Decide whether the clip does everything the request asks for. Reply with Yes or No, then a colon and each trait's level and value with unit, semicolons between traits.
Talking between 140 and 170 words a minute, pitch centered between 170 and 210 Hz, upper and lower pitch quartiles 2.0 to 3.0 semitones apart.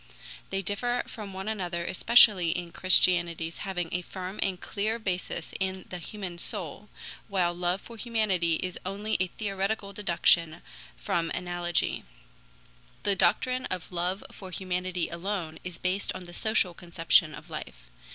Yes: average, 145 wpm; medium, 185 Hz; narrow, 2.5 semitones